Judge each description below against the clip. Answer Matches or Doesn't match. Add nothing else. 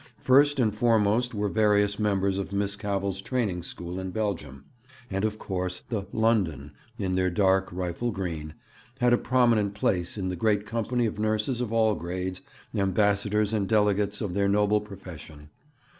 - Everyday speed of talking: Matches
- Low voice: Matches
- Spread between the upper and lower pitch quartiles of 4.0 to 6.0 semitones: Doesn't match